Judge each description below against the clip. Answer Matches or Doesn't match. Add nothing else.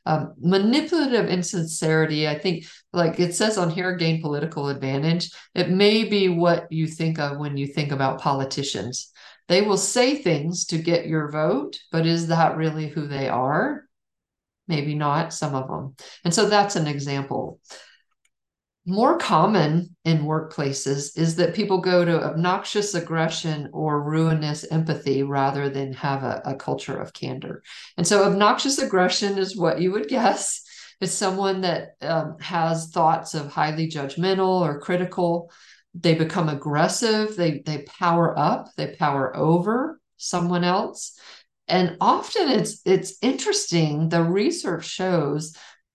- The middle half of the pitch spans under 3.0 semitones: Doesn't match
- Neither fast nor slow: Matches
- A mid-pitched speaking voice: Matches